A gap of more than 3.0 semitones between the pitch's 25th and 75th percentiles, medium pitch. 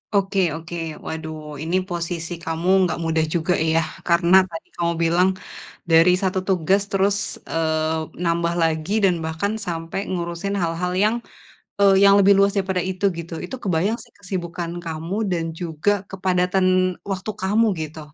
No: average, 2.7 semitones; medium, 175 Hz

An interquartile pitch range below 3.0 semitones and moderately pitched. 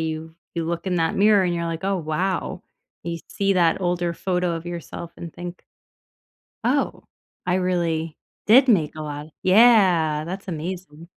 Yes: narrow, 2.6 semitones; medium, 175 Hz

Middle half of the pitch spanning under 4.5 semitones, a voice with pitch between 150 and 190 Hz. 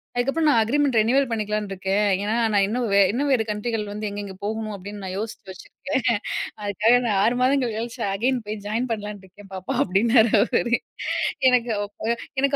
No: average, 3.2 semitones; high, 220 Hz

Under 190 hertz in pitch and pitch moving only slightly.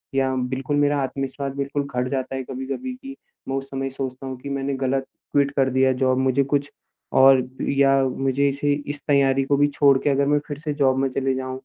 Yes: low, 135 Hz; narrow, 1.1 semitones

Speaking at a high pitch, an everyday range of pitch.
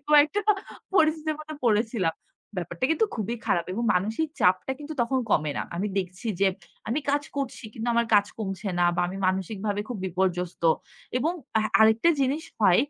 No: high, 220 Hz; wide, 7.0 semitones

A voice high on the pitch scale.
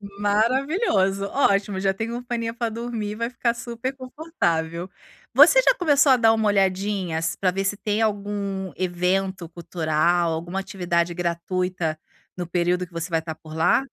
Yes: high, 195 Hz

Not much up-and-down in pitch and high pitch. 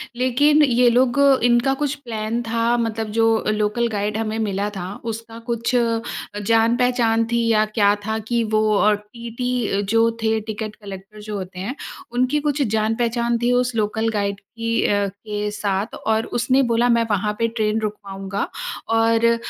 Yes: narrow, 2.1 semitones; high, 225 Hz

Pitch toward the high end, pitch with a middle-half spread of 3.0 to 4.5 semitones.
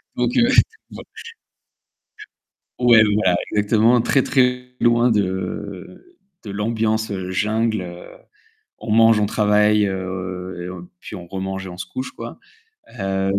No: low, 105 Hz; average, 3.4 semitones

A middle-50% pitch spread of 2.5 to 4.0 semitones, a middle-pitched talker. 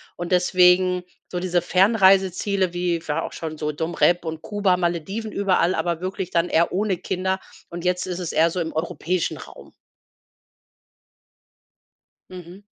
No: narrow, 1.7 semitones; medium, 180 Hz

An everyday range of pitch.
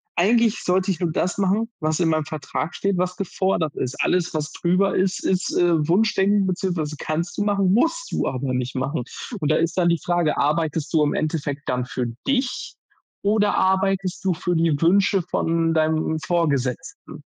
Yes: average, 3.6 semitones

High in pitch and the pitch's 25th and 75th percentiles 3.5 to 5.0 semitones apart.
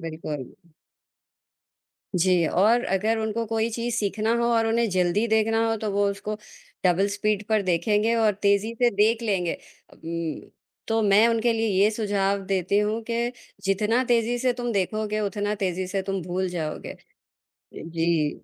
No: high, 210 Hz; average, 3.1 semitones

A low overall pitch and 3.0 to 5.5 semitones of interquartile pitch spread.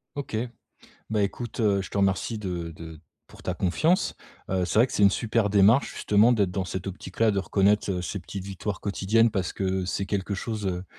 No: low, 100 Hz; narrow, 2.4 semitones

